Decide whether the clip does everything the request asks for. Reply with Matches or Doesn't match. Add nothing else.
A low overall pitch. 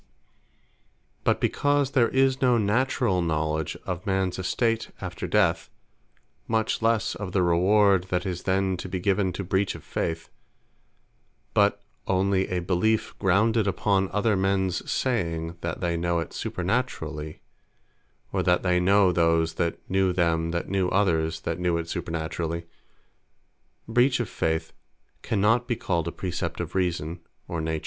Matches